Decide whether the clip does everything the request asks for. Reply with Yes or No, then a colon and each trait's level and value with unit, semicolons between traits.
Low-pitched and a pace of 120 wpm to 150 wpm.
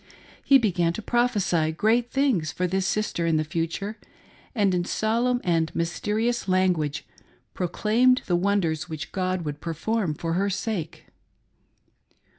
No: medium, 185 Hz; average, 145 wpm